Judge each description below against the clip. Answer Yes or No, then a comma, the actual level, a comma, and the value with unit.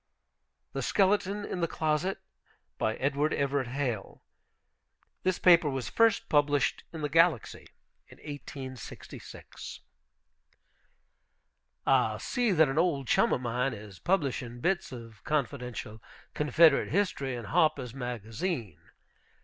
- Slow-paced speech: Yes, slow, 115 wpm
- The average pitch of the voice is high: No, medium, 140 Hz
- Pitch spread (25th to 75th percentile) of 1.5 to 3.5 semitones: No, average, 5.3 semitones